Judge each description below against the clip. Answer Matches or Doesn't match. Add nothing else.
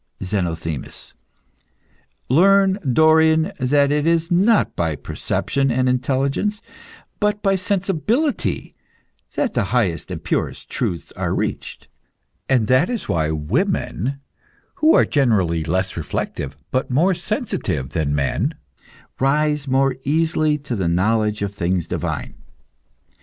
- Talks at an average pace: Doesn't match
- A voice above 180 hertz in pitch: Doesn't match